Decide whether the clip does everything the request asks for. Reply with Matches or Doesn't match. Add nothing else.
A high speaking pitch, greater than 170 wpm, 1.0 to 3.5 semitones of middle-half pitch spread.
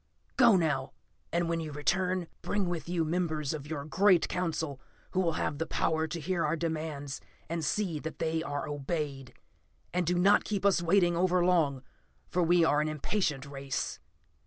Doesn't match